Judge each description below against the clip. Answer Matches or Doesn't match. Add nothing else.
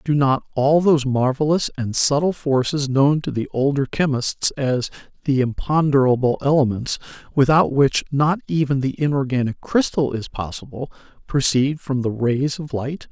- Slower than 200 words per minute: Matches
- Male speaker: Matches